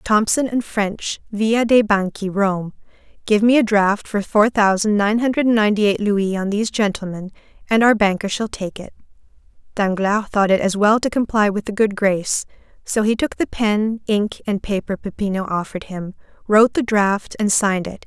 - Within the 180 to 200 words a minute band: Yes, average, 185 wpm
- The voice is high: Yes, high, 210 Hz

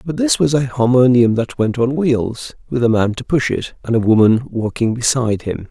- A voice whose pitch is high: No, low, 120 Hz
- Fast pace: Yes, fast, 220 wpm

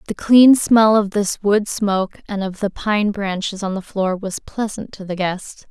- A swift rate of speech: Yes, fast, 210 wpm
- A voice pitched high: Yes, high, 200 Hz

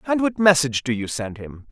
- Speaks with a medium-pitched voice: Yes, medium, 145 Hz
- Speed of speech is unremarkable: No, fast, 245 wpm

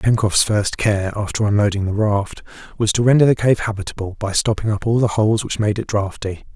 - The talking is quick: Yes, fast, 210 wpm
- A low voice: Yes, low, 105 Hz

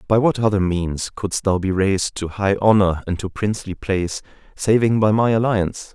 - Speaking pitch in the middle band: No, low, 100 Hz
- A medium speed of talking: Yes, average, 190 wpm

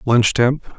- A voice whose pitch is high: No, low, 125 Hz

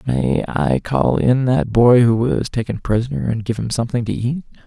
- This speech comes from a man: Yes, male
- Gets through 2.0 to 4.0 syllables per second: No, 4.9 syllables/s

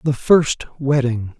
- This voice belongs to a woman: No, male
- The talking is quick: No, slow, 130 wpm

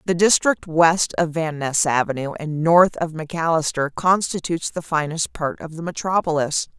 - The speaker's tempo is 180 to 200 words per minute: No, average, 160 wpm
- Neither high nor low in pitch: Yes, medium, 165 Hz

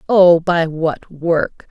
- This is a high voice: No, medium, 170 Hz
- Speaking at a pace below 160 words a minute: Yes, average, 140 wpm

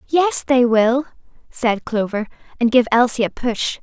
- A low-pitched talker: No, high, 245 Hz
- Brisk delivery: No, average, 155 wpm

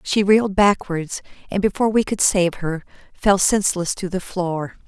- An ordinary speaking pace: Yes, average, 170 wpm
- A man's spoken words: No, female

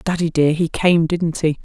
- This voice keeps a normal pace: No, fast, 220 wpm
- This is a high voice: No, medium, 165 Hz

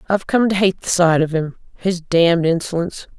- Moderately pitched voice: Yes, medium, 175 Hz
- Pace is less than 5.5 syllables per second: No, 5.8 syllables/s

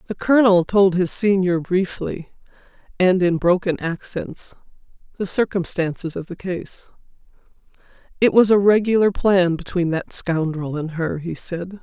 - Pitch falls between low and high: Yes, medium, 180 Hz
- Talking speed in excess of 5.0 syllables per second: No, 4.4 syllables/s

